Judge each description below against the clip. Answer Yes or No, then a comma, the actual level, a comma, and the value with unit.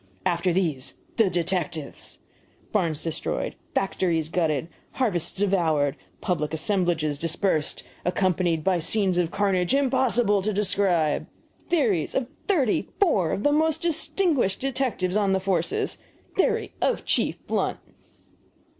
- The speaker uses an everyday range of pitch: Yes, average, 4.8 semitones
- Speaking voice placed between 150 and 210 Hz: Yes, medium, 185 Hz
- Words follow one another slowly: Yes, slow, 120 wpm